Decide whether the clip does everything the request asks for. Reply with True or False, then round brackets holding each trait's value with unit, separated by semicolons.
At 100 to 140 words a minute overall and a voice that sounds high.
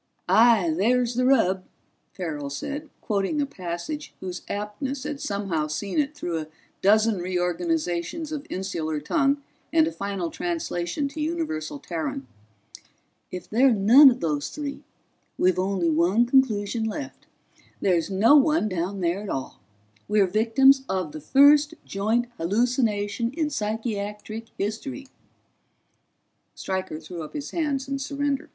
True (135 wpm; 210 Hz)